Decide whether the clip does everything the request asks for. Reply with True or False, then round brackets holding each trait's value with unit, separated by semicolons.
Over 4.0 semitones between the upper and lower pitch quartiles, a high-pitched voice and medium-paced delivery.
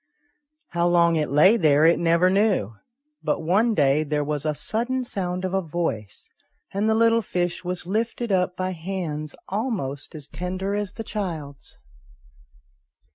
False (4.7 semitones; 180 Hz; 155 wpm)